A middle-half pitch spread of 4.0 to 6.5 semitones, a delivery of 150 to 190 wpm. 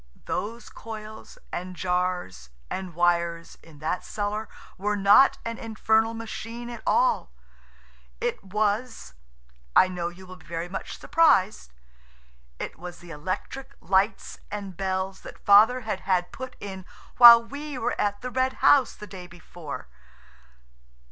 No: average, 4.6 semitones; slow, 135 wpm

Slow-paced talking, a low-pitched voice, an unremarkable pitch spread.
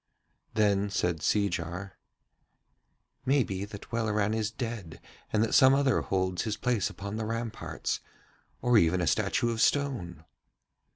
Yes: slow, 130 wpm; low, 105 Hz; average, 3.9 semitones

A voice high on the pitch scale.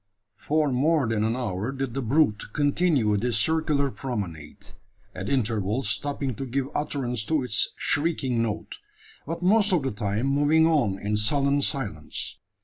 No: low, 130 Hz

